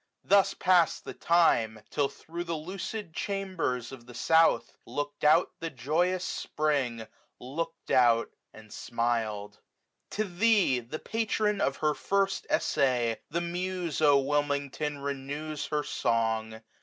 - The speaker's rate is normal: No, slow, 130 wpm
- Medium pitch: Yes, medium, 150 Hz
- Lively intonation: Yes, wide, 5.8 semitones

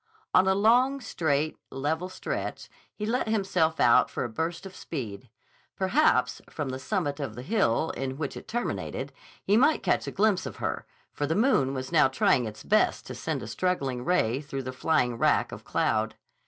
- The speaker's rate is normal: Yes, average, 190 wpm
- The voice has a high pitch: No, medium, 160 Hz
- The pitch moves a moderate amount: No, wide, 6.9 semitones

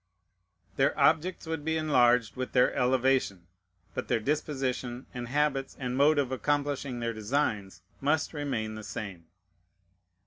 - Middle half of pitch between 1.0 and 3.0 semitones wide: No, average, 3.5 semitones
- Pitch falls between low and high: No, low, 130 Hz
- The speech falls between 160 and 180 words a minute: No, slow, 135 wpm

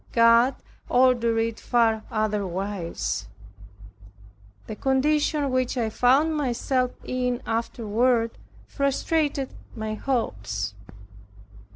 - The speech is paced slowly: Yes, slow, 80 wpm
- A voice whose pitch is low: No, high, 240 Hz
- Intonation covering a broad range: No, average, 3.2 semitones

